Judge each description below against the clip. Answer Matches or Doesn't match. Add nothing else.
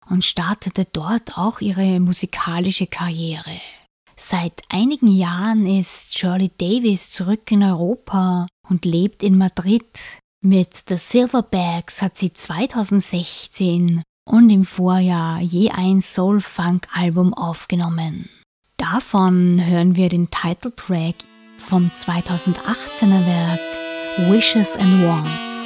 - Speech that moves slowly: Matches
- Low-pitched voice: Doesn't match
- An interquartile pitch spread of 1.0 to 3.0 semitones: Matches